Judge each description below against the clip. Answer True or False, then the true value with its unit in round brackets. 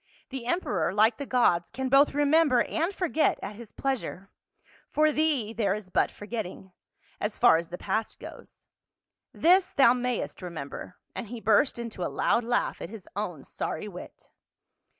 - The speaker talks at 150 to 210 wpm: True (170 wpm)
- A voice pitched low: False (235 Hz)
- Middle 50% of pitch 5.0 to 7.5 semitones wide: True (5.4 semitones)